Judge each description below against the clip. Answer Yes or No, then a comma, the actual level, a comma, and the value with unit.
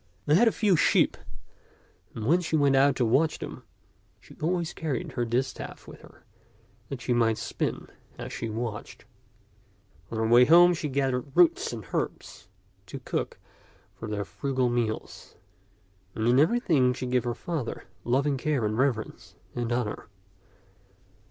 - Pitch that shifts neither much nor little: Yes, average, 4.4 semitones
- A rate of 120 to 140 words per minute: No, average, 155 wpm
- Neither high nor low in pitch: No, low, 130 Hz